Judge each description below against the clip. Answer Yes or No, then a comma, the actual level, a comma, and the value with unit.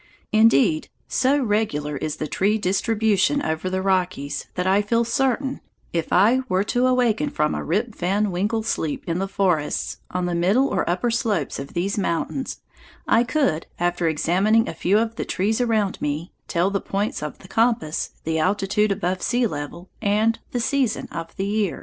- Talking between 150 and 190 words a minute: Yes, average, 180 wpm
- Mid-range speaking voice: No, high, 200 Hz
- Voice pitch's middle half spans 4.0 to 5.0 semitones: Yes, average, 4.7 semitones